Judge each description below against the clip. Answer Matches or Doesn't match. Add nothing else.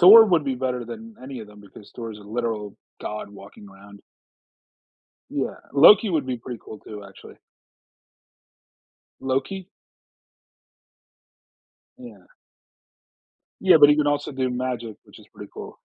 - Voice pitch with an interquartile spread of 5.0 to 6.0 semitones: Matches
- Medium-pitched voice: Doesn't match